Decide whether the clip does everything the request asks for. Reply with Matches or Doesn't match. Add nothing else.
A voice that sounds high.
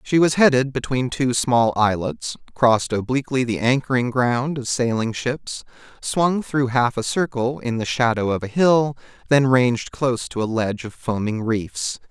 Doesn't match